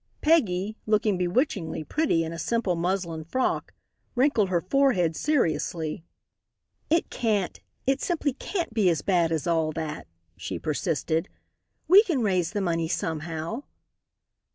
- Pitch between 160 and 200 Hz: Yes, medium, 185 Hz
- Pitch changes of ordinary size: No, wide, 7.2 semitones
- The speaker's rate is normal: No, slow, 130 wpm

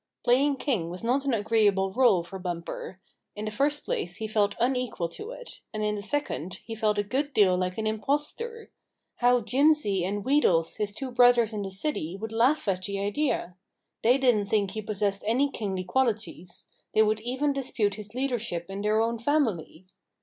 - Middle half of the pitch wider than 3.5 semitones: Yes, average, 4.6 semitones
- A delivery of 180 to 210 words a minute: Yes, average, 190 wpm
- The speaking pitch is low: No, high, 215 Hz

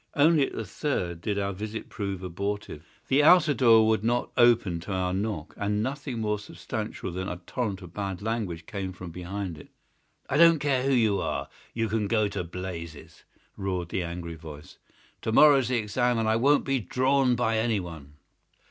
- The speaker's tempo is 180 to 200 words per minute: Yes, average, 185 wpm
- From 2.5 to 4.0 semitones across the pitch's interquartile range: No, average, 5.0 semitones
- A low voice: Yes, low, 105 Hz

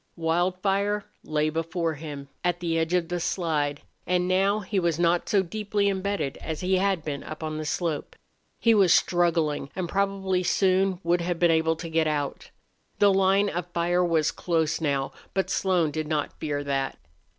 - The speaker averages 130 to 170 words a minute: No, average, 180 wpm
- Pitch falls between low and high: Yes, medium, 175 Hz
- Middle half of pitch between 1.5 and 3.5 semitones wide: Yes, average, 3.2 semitones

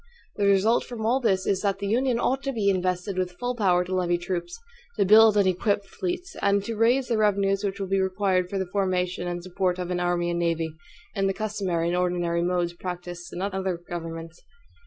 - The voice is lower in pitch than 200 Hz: Yes, high, 190 Hz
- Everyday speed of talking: No, fast, 215 wpm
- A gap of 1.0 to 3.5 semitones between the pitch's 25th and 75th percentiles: Yes, narrow, 2.6 semitones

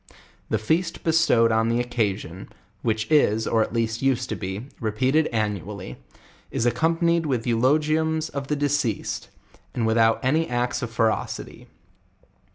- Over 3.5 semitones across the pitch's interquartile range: Yes, average, 5.1 semitones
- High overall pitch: No, low, 120 Hz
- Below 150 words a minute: Yes, average, 140 wpm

